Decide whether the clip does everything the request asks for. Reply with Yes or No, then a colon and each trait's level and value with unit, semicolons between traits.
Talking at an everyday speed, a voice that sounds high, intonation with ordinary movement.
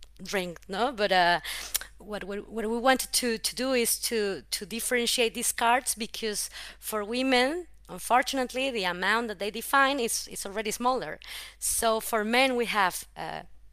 Yes: average, 160 wpm; high, 225 Hz; average, 3.4 semitones